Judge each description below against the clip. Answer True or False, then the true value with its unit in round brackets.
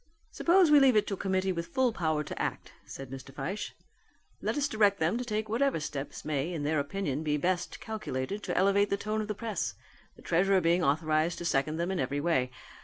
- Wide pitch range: True (5.8 semitones)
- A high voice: False (180 Hz)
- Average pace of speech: False (220 wpm)